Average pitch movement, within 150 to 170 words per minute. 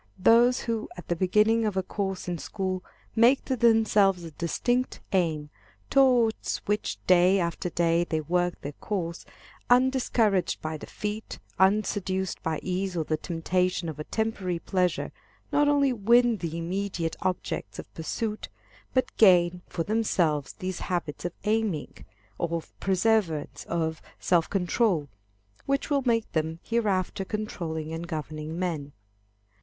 No: average, 4.7 semitones; average, 140 wpm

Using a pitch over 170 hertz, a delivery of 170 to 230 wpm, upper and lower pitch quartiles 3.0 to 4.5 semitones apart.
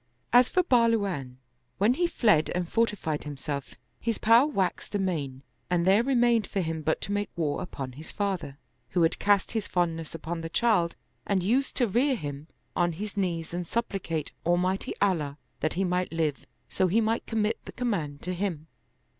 No: medium, 185 Hz; average, 180 wpm; average, 5.3 semitones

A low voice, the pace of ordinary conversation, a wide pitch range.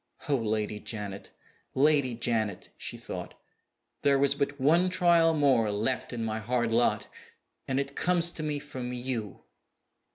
No: low, 130 Hz; average, 150 wpm; average, 4.5 semitones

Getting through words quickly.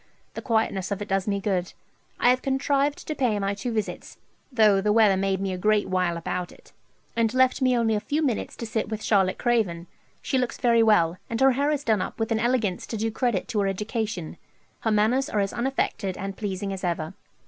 Yes: fast, 225 wpm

